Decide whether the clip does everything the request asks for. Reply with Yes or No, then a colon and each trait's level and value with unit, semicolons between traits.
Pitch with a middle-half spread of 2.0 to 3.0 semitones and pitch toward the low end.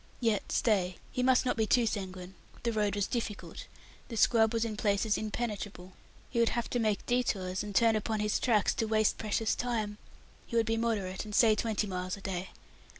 No: narrow, 2.4 semitones; high, 215 Hz